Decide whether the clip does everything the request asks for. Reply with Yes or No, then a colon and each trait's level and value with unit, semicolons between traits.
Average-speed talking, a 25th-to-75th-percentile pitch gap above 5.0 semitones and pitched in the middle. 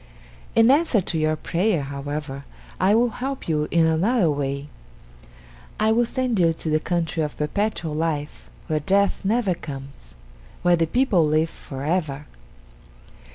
Yes: average, 150 wpm; wide, 5.5 semitones; medium, 165 Hz